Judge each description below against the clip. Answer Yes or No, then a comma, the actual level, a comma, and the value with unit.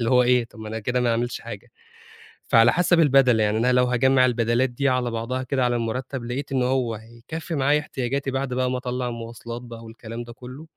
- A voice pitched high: No, low, 125 Hz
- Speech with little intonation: Yes, narrow, 2.0 semitones